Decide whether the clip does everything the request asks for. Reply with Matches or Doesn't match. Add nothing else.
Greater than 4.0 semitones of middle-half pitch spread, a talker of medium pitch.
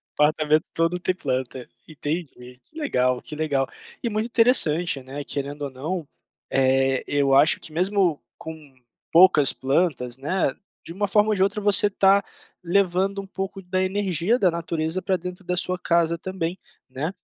Matches